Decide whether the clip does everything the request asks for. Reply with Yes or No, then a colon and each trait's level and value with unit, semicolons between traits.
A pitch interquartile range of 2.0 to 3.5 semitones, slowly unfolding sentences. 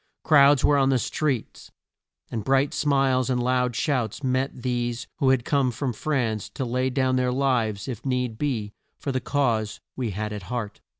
No: narrow, 2.5 semitones; average, 180 wpm